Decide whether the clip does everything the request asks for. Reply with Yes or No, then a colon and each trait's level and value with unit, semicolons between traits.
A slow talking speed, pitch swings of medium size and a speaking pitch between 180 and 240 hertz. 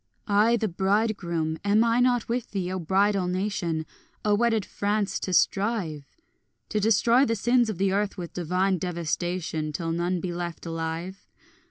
No: average, 160 wpm; average, 3.7 semitones; high, 190 Hz